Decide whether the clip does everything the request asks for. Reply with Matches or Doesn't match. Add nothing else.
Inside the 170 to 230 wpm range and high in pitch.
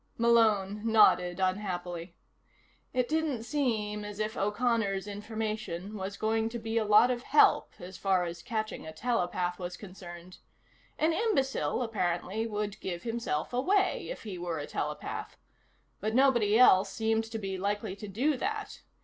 Doesn't match